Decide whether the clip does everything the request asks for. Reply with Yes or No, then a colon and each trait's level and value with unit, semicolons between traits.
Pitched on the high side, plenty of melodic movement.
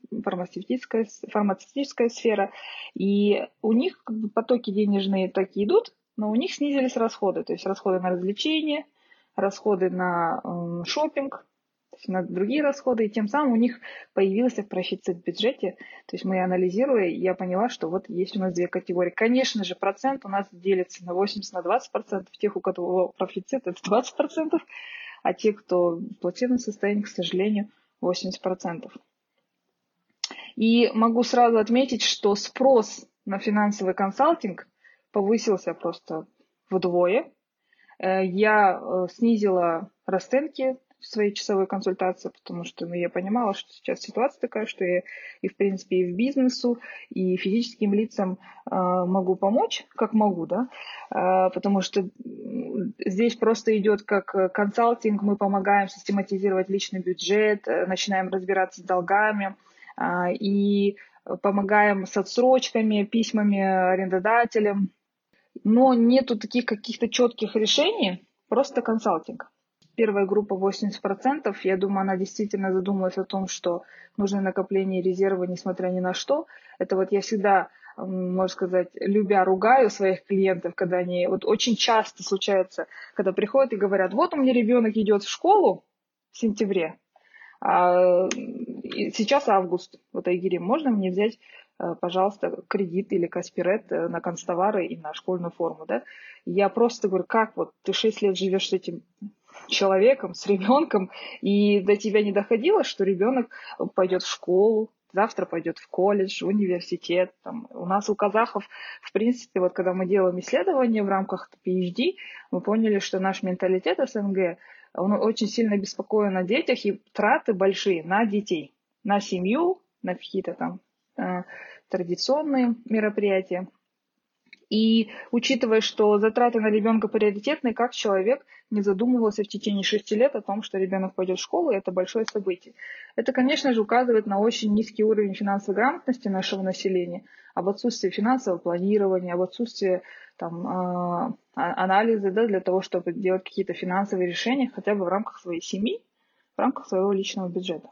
No: high, 200 Hz; average, 3.6 semitones